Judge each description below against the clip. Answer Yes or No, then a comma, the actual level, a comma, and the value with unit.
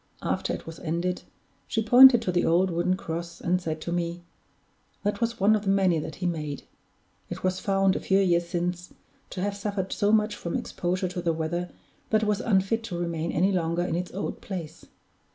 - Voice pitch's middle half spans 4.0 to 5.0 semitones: No, average, 2.7 semitones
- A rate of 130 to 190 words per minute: No, fast, 205 wpm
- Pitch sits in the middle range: Yes, medium, 180 Hz